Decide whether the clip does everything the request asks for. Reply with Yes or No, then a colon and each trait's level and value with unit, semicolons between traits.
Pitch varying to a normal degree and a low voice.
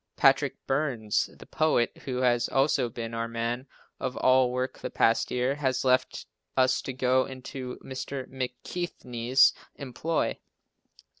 No: narrow, 1.6 semitones; low, 130 Hz